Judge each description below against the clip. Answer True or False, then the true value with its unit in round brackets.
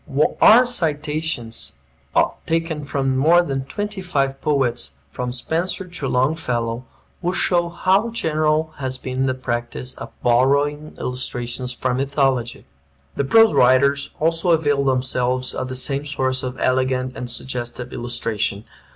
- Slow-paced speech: True (130 wpm)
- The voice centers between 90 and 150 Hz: True (135 Hz)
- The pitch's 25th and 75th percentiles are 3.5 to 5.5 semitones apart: True (3.8 semitones)